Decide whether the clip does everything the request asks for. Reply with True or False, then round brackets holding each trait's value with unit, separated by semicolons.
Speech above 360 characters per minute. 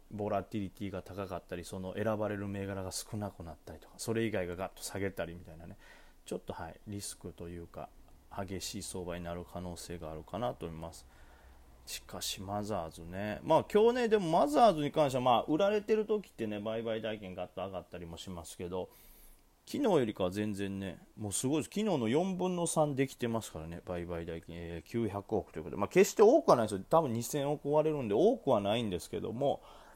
True (420 characters per minute)